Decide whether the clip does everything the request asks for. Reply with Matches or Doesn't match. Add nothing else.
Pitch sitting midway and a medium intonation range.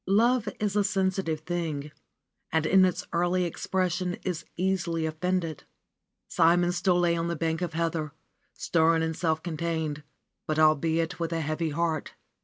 Doesn't match